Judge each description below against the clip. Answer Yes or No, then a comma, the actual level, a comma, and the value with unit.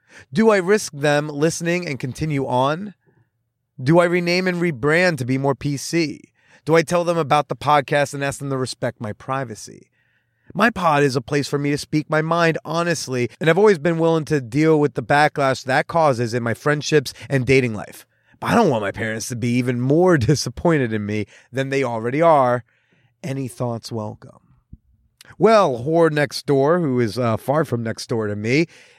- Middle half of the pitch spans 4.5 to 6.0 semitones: Yes, average, 4.8 semitones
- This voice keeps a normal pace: Yes, average, 195 wpm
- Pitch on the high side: No, medium, 140 Hz